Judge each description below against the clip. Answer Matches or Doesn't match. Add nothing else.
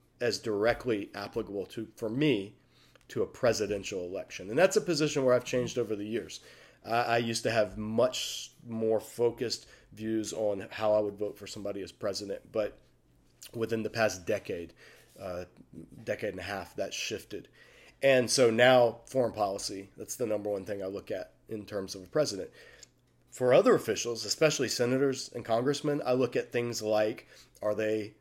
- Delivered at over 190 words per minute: Doesn't match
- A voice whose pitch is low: Matches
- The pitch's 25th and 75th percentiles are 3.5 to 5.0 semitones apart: Doesn't match